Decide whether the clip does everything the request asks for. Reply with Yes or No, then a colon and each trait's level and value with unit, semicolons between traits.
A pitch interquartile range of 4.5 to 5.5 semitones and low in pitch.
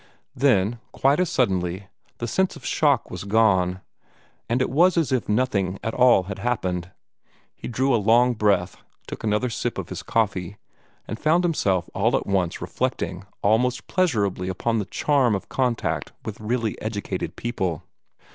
Yes: average, 4.8 semitones; low, 110 Hz